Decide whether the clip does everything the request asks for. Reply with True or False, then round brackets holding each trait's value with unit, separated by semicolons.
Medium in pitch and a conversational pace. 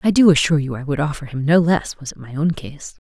False (150 Hz; 295 wpm)